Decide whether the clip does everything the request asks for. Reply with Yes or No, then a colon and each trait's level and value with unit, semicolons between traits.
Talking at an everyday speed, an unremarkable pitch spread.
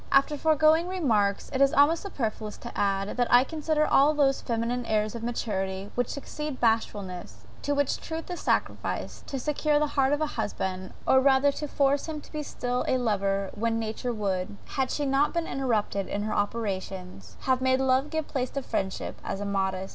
No: average, 195 wpm; wide, 5.8 semitones